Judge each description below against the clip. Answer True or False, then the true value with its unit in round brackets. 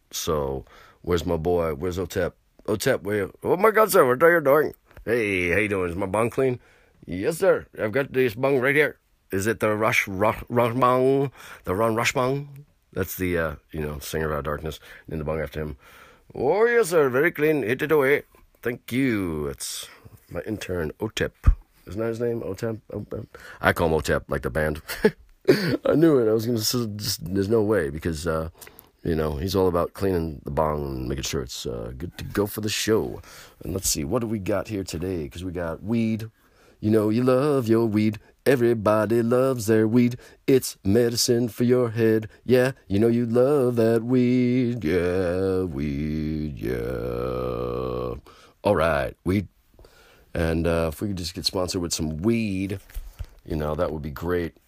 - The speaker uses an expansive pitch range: True (6.4 semitones)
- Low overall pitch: True (100 Hz)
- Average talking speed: True (190 wpm)